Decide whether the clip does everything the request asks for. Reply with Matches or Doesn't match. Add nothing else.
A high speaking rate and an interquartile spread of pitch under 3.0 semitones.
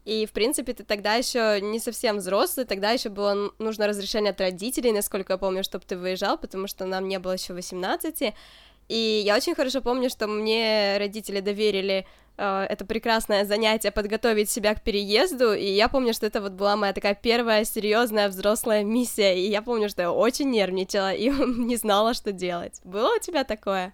Matches